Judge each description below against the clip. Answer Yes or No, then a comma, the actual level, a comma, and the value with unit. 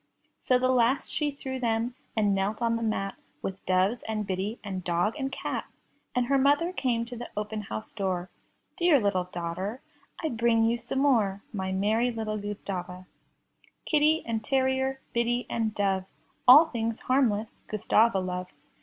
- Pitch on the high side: Yes, high, 225 Hz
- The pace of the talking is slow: No, average, 165 wpm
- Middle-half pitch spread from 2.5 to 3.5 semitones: No, average, 4.4 semitones